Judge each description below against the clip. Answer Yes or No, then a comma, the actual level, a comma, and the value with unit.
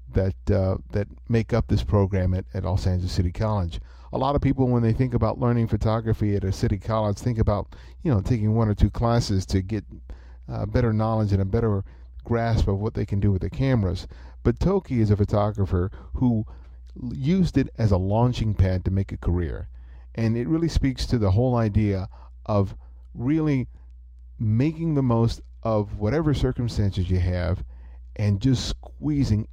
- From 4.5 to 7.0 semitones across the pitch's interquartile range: No, average, 4.0 semitones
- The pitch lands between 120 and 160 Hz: No, low, 105 Hz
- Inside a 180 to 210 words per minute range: Yes, average, 185 wpm